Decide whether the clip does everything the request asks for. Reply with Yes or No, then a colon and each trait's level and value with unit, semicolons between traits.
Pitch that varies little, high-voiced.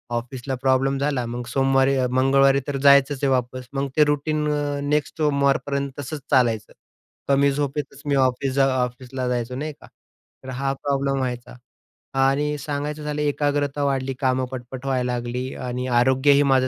No: narrow, 1.8 semitones; low, 135 Hz